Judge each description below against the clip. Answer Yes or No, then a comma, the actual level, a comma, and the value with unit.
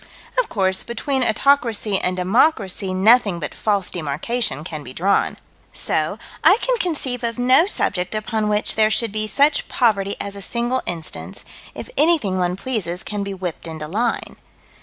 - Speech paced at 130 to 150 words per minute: No, average, 160 wpm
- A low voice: No, high, 210 Hz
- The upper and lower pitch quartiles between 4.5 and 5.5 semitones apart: Yes, average, 4.8 semitones